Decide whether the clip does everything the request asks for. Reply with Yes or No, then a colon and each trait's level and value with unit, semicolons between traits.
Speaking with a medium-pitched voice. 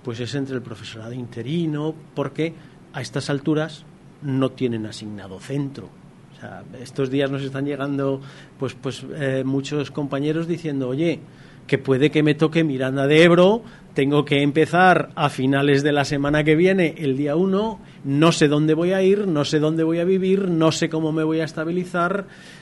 Yes: medium, 150 Hz